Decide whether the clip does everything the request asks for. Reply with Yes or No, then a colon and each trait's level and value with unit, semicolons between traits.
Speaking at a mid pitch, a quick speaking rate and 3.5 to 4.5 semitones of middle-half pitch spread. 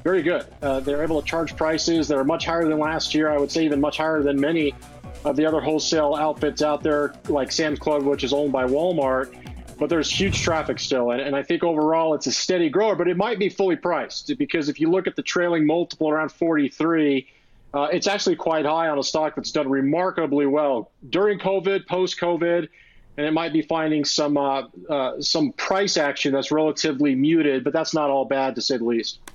No: medium, 155 Hz; fast, 220 wpm; narrow, 2.6 semitones